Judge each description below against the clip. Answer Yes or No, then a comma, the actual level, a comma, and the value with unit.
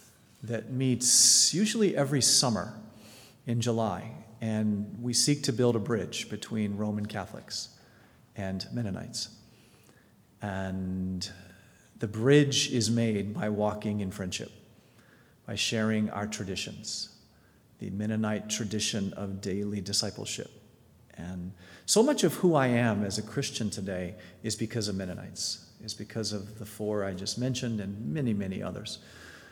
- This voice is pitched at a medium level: No, low, 110 Hz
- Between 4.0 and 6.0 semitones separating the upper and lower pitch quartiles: No, average, 2.9 semitones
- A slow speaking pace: Yes, slow, 130 wpm